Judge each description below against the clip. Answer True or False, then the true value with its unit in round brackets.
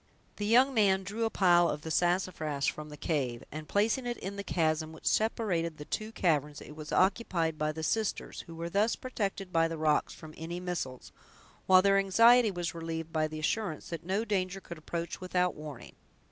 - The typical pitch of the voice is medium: True (175 Hz)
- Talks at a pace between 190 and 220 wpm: True (200 wpm)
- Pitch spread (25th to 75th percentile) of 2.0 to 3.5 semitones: False (4.2 semitones)